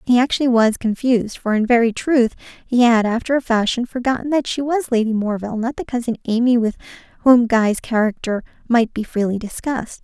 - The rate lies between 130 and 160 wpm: No, average, 185 wpm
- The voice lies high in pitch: Yes, high, 235 Hz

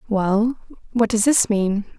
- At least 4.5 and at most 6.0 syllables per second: No, 3.7 syllables/s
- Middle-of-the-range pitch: No, high, 220 Hz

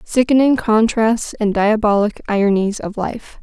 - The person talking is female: Yes, female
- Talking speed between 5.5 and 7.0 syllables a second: No, 4.4 syllables/s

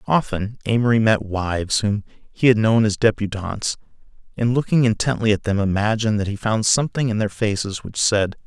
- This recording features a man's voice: Yes, male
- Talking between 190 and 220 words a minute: No, average, 175 wpm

